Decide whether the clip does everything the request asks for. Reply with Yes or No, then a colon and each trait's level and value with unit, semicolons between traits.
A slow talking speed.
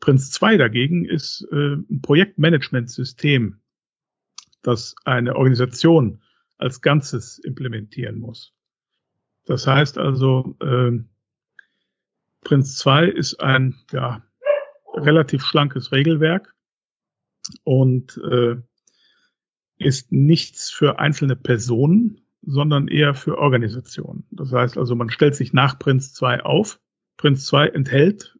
Yes: slow, 105 wpm